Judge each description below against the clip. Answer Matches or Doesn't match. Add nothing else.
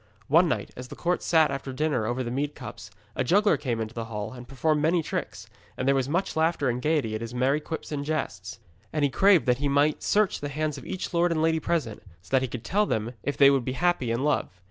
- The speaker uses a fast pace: Matches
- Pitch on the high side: Doesn't match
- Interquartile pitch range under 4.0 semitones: Doesn't match